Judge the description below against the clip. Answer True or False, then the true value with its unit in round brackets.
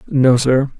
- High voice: False (130 Hz)